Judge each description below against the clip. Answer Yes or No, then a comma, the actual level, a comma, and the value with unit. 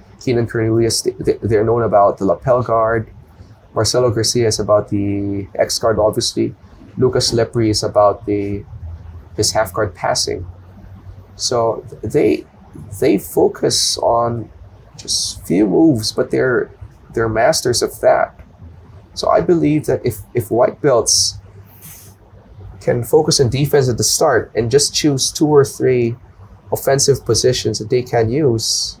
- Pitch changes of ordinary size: Yes, average, 3.4 semitones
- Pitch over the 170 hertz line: No, low, 110 Hz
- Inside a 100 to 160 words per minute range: Yes, average, 140 wpm